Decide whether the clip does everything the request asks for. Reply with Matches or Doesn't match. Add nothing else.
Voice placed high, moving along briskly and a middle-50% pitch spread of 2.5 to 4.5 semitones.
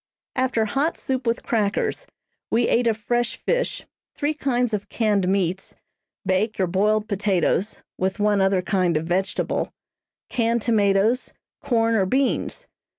Doesn't match